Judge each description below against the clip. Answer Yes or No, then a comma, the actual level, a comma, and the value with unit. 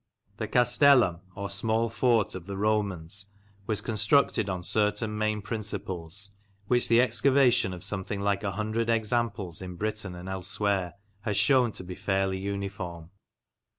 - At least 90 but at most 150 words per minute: Yes, average, 145 wpm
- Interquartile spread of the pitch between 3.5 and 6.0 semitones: No, average, 2.7 semitones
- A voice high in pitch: No, low, 100 Hz